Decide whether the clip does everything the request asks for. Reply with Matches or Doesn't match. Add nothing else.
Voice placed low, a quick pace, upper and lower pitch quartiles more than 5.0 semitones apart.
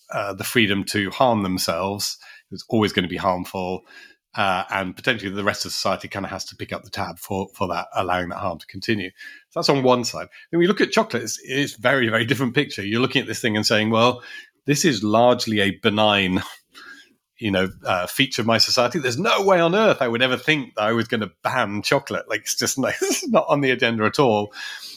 Matches